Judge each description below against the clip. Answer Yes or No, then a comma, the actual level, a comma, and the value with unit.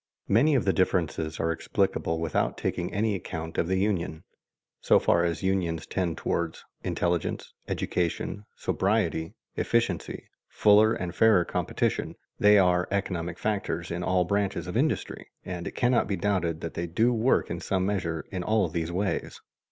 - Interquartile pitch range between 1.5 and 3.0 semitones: No, average, 3.4 semitones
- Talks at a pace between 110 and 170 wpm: Yes, average, 160 wpm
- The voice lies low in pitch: Yes, very low, 90 Hz